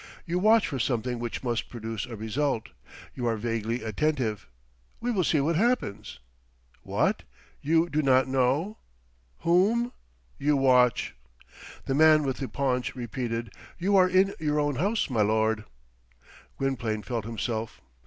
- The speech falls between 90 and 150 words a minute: Yes, average, 145 wpm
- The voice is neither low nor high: No, low, 130 Hz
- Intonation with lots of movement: Yes, wide, 5.7 semitones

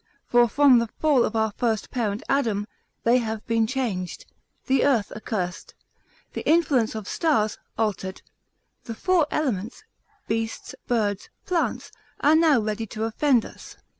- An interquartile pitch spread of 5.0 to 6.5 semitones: No, average, 4.1 semitones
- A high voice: Yes, high, 230 Hz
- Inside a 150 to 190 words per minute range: No, average, 140 wpm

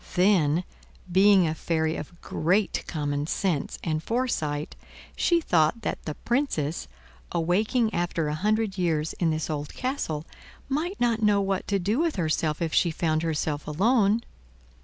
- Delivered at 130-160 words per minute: Yes, average, 150 wpm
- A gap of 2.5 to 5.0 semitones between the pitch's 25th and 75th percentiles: No, wide, 5.6 semitones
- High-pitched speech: No, medium, 175 Hz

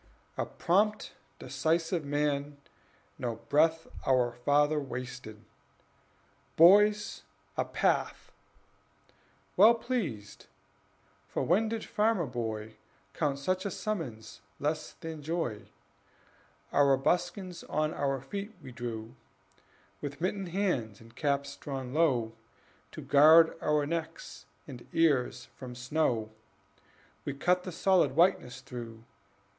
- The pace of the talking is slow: Yes, slow, 110 wpm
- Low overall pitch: No, medium, 145 Hz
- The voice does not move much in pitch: No, wide, 5.6 semitones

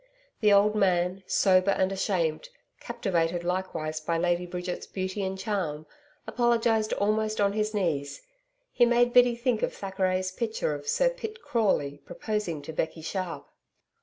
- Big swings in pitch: No, average, 3.8 semitones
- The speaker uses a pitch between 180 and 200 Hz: Yes, high, 190 Hz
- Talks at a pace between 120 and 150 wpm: Yes, average, 145 wpm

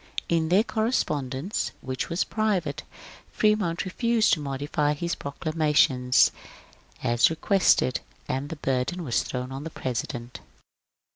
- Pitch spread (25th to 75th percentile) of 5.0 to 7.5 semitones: Yes, wide, 5.4 semitones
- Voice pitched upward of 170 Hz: No, medium, 155 Hz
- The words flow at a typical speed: No, slow, 125 wpm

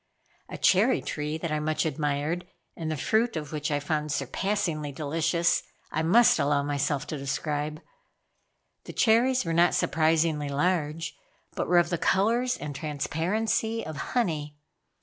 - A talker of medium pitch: Yes, medium, 155 Hz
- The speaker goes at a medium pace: Yes, average, 150 wpm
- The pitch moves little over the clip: No, average, 3.4 semitones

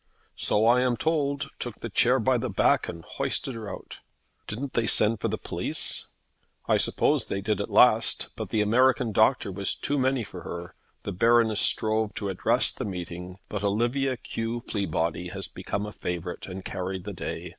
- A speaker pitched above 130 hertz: No, low, 110 Hz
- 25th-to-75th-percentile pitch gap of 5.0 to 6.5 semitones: No, average, 4.1 semitones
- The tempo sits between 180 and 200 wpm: Yes, average, 185 wpm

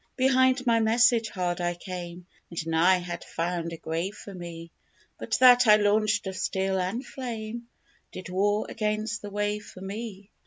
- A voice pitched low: No, high, 205 Hz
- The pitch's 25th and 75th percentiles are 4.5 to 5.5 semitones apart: No, average, 3.9 semitones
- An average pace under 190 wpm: Yes, average, 165 wpm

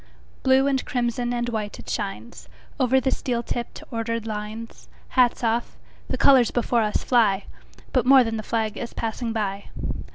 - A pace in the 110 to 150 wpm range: Yes, average, 140 wpm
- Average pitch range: No, narrow, 2.1 semitones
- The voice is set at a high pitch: Yes, high, 235 Hz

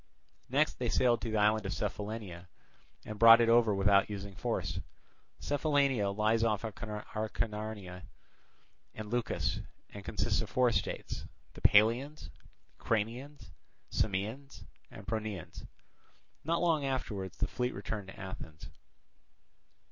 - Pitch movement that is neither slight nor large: Yes, average, 3.2 semitones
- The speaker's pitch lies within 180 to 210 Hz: No, low, 110 Hz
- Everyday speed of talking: No, slow, 120 wpm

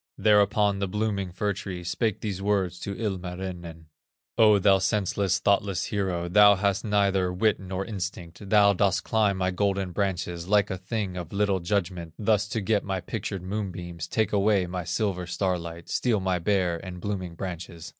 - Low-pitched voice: Yes, very low, 95 Hz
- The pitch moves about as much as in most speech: No, narrow, 2.3 semitones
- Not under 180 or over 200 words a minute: No, average, 165 wpm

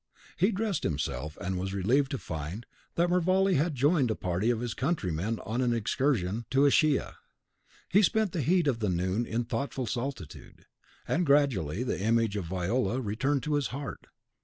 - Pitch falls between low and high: No, low, 120 Hz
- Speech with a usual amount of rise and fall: No, wide, 6.9 semitones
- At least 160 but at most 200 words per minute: Yes, average, 170 wpm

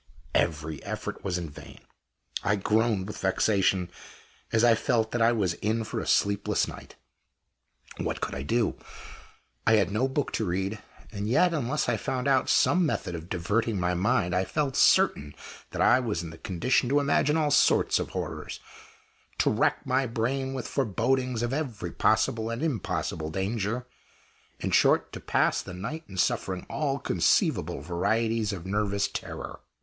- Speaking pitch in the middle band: No, low, 110 Hz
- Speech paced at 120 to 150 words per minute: No, average, 165 wpm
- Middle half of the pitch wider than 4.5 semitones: Yes, average, 5.2 semitones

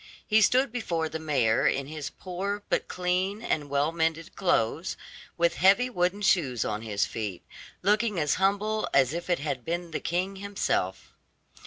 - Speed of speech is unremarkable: Yes, average, 165 wpm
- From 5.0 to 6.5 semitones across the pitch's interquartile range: Yes, wide, 5.4 semitones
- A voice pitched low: No, medium, 170 Hz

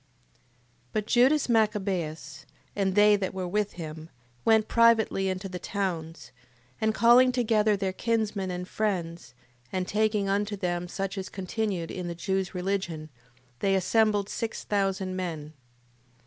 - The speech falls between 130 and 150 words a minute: Yes, average, 140 wpm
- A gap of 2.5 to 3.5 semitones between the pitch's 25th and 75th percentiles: Yes, average, 3.0 semitones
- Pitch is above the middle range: Yes, high, 195 Hz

